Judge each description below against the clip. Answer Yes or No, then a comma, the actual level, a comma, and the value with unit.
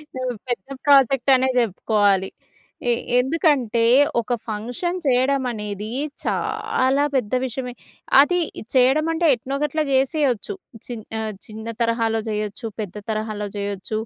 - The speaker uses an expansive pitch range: No, average, 3.9 semitones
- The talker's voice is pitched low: No, high, 245 Hz